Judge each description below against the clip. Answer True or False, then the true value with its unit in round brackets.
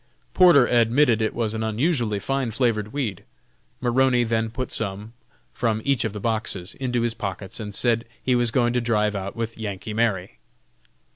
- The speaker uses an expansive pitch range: False (2.5 semitones)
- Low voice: True (115 Hz)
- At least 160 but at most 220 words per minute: True (170 wpm)